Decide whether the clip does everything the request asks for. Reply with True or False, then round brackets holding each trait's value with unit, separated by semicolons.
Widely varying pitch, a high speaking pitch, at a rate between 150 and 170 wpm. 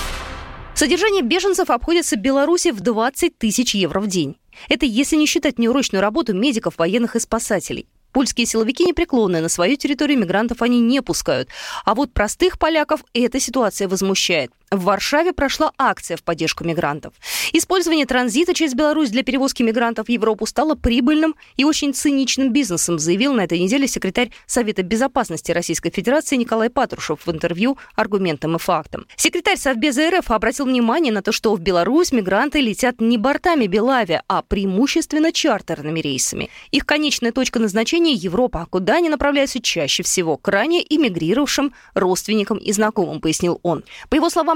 True (7.1 semitones; 240 Hz; 155 wpm)